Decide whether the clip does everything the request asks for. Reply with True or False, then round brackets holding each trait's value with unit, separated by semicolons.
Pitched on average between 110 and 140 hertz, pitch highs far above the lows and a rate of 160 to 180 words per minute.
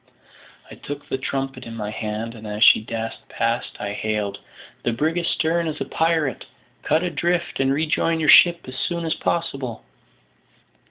True (135 Hz; 6.2 semitones; 165 wpm)